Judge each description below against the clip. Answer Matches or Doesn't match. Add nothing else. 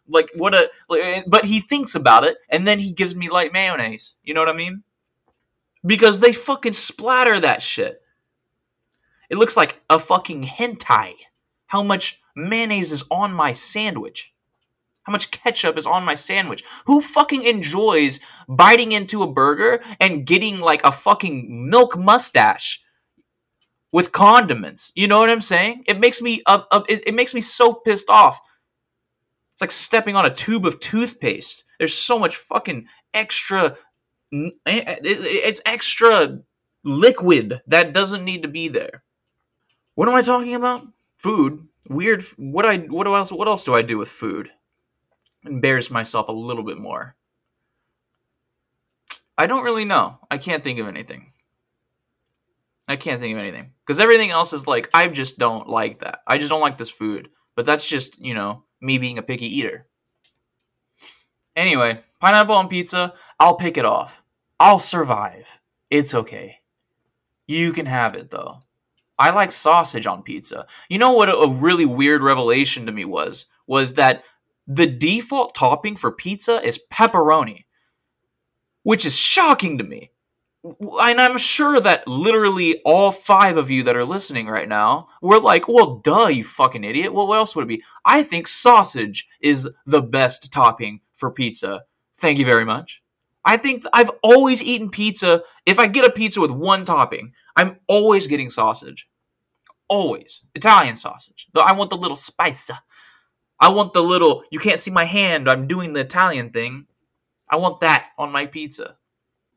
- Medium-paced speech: Matches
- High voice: Doesn't match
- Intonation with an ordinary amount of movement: Doesn't match